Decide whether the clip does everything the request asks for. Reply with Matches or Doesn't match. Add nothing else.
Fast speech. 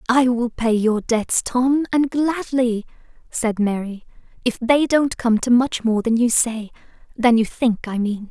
Doesn't match